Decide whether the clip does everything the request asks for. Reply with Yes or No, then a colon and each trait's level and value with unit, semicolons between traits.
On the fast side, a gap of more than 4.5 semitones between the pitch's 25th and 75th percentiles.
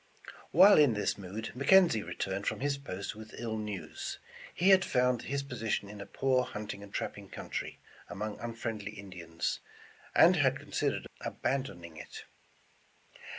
No: average, 150 wpm; average, 5.1 semitones